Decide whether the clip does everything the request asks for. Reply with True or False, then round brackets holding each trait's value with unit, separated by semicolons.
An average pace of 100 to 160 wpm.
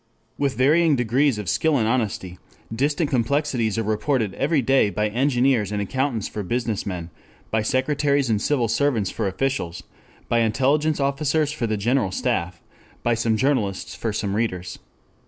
True (155 wpm)